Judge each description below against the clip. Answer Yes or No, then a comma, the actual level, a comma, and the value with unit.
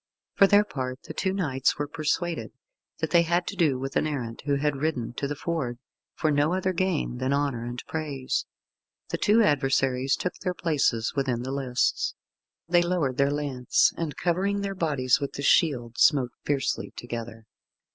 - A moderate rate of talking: Yes, average, 175 wpm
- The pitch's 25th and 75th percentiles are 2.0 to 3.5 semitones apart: No, average, 4.8 semitones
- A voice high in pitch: No, medium, 145 Hz